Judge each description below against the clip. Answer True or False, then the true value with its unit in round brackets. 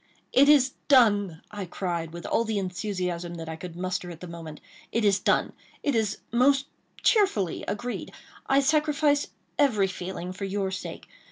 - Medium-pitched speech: False (200 Hz)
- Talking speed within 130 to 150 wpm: False (160 wpm)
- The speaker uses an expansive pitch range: True (6.3 semitones)